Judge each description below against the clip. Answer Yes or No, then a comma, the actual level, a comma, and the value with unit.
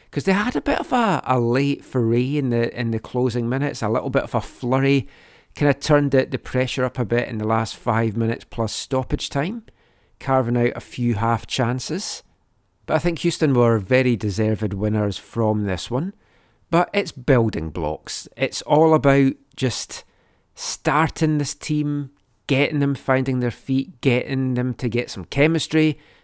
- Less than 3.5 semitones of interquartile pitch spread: No, average, 3.8 semitones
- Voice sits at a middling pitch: No, low, 130 Hz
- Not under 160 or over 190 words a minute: Yes, average, 180 wpm